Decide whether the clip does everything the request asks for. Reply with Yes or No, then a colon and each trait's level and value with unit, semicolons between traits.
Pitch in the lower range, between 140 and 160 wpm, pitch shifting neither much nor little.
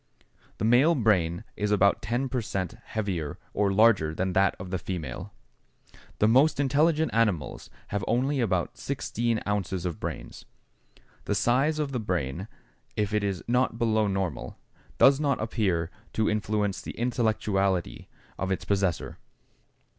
Yes: low, 105 Hz; average, 145 wpm; average, 4.2 semitones